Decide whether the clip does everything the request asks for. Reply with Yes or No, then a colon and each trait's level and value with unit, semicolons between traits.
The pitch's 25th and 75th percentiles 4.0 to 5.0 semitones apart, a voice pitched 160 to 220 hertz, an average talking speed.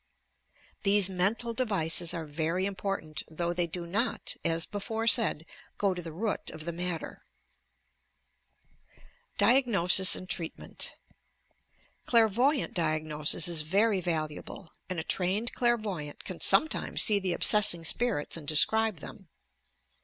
No: average, 4.5 semitones; medium, 185 Hz; slow, 125 wpm